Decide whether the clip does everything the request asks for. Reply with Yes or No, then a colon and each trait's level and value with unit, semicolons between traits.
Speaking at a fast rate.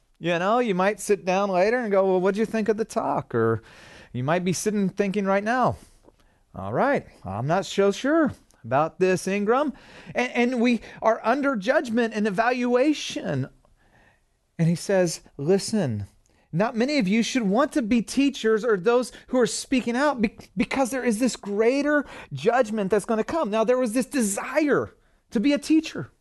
No: average, 185 wpm